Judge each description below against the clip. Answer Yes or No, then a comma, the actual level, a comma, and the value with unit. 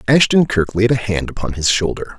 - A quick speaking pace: Yes, fast, 220 wpm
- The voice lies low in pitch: Yes, low, 105 Hz